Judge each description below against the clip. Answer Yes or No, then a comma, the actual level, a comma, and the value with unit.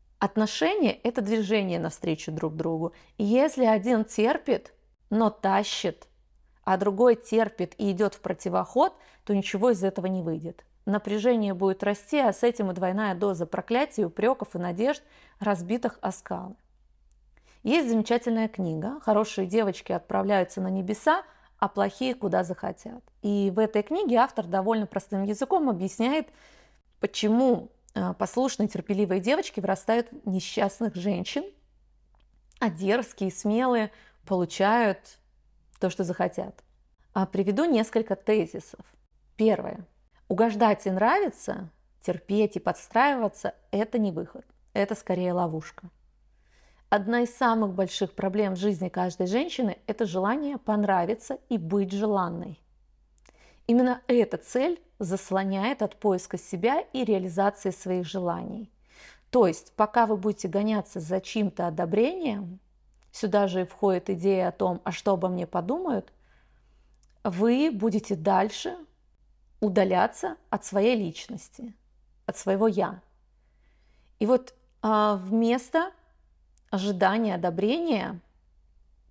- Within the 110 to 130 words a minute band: Yes, average, 120 wpm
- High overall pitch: Yes, high, 205 Hz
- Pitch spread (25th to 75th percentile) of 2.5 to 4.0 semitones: Yes, average, 3.5 semitones